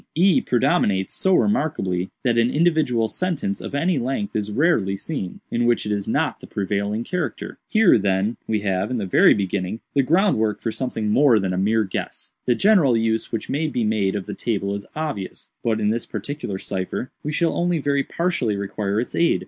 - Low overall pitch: Yes, low, 115 Hz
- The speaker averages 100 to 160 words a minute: No, average, 195 wpm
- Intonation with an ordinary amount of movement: No, wide, 6.8 semitones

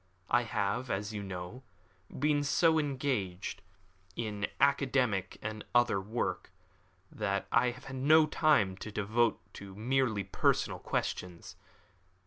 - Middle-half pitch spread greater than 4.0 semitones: Yes, average, 5.1 semitones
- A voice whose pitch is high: No, low, 115 Hz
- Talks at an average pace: No, slow, 120 wpm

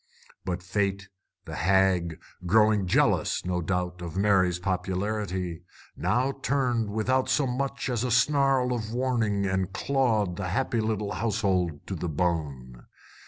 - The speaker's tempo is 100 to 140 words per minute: Yes, slow, 135 wpm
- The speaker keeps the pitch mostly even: No, average, 5.0 semitones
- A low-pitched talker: Yes, low, 100 Hz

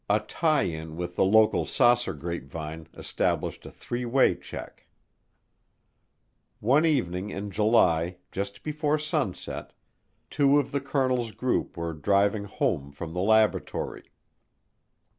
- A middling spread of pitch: No, wide, 6.9 semitones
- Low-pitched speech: Yes, low, 105 Hz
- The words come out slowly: Yes, slow, 125 wpm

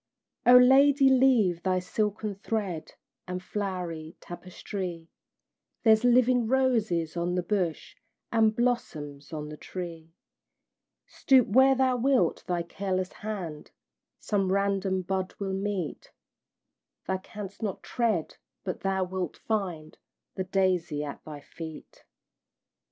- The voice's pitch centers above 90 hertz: Yes, high, 190 Hz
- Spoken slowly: Yes, slow, 120 wpm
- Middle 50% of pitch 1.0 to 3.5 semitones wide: No, average, 4.3 semitones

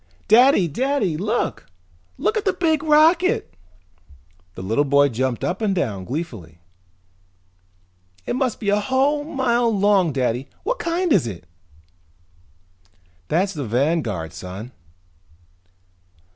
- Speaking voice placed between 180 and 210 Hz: Yes, high, 190 Hz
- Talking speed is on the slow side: Yes, slow, 115 wpm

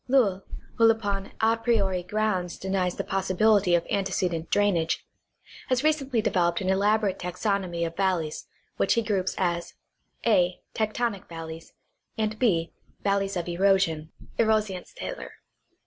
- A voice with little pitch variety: No, average, 3.5 semitones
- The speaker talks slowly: Yes, slow, 130 wpm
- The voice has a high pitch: Yes, high, 195 Hz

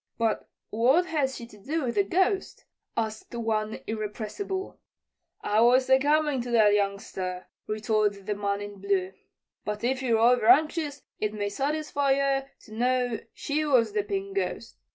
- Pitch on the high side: Yes, high, 235 Hz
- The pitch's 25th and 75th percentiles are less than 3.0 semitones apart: No, average, 5.2 semitones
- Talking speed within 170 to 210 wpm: No, average, 155 wpm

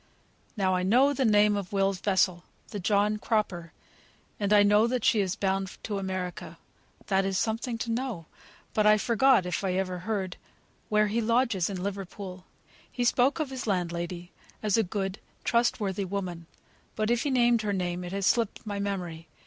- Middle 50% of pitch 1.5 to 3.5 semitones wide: Yes, average, 3.2 semitones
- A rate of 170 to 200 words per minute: Yes, average, 180 wpm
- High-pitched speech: Yes, high, 200 Hz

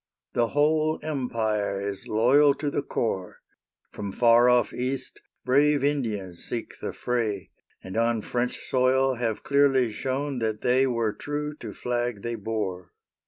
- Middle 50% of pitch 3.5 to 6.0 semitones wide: Yes, average, 3.8 semitones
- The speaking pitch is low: Yes, low, 120 Hz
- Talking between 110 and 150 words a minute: Yes, average, 145 wpm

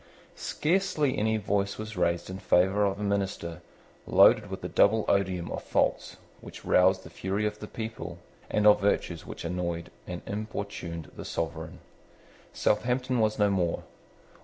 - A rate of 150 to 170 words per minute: Yes, average, 155 wpm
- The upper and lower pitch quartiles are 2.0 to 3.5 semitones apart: Yes, average, 3.1 semitones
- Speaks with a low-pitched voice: Yes, low, 100 Hz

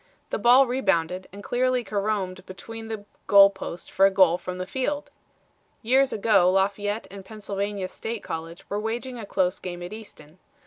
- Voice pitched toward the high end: Yes, high, 200 Hz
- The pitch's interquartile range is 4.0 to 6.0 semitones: No, average, 3.3 semitones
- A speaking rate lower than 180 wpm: Yes, average, 170 wpm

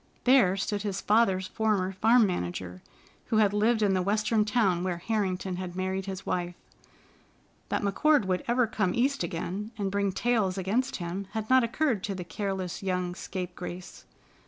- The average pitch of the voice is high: Yes, high, 195 Hz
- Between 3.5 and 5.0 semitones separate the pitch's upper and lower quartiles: No, average, 3.0 semitones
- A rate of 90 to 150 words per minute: No, average, 170 wpm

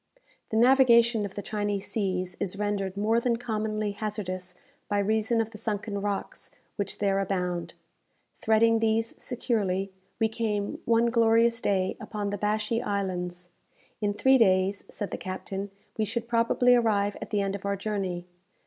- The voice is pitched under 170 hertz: No, high, 210 Hz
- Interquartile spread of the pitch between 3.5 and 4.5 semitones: No, narrow, 2.5 semitones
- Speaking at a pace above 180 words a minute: No, average, 155 wpm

